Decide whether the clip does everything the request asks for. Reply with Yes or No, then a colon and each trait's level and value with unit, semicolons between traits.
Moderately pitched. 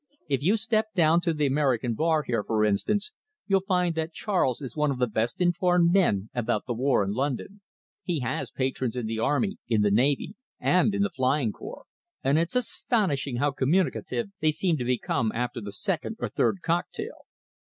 Yes: medium, 145 Hz